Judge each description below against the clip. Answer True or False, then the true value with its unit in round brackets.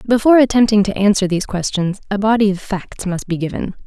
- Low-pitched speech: False (205 Hz)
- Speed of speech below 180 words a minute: False (200 wpm)